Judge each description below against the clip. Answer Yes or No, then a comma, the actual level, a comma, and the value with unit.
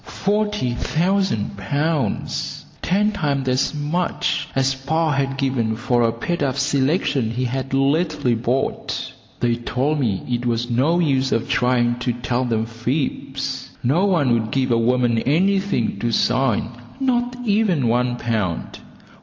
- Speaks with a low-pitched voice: Yes, low, 130 Hz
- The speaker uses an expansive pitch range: No, average, 4.5 semitones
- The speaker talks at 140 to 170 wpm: Yes, average, 145 wpm